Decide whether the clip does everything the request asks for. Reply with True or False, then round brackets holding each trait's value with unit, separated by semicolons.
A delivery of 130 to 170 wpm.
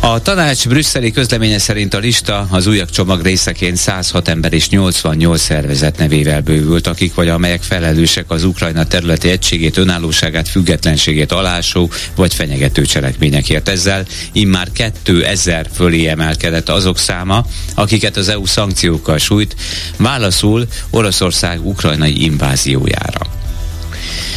False (120 wpm)